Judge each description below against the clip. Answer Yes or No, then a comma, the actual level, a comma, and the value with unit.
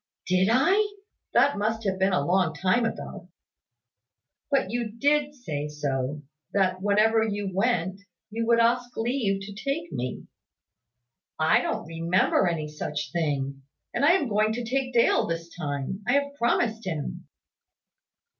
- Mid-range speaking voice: No, high, 205 Hz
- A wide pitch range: Yes, wide, 6.5 semitones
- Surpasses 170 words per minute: No, average, 145 wpm